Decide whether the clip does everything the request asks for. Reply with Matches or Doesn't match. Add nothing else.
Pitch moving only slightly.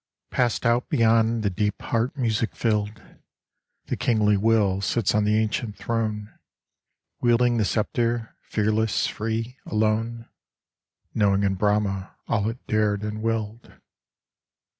Matches